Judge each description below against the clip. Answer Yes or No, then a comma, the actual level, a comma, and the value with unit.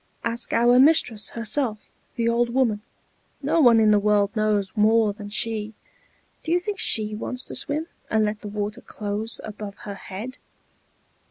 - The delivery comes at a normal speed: Yes, average, 165 wpm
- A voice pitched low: No, high, 220 Hz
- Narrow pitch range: Yes, narrow, 2.3 semitones